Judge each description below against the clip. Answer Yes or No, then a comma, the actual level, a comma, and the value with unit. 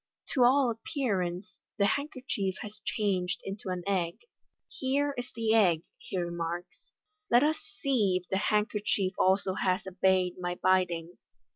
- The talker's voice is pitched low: No, high, 195 Hz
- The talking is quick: No, average, 155 wpm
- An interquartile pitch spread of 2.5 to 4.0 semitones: No, average, 4.9 semitones